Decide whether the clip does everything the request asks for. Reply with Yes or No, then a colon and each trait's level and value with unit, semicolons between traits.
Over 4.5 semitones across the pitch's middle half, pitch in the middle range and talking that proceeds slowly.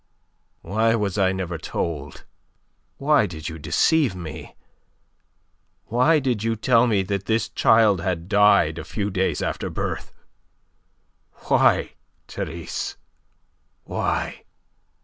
No: average, 5.1 semitones; low, 100 Hz; slow, 110 wpm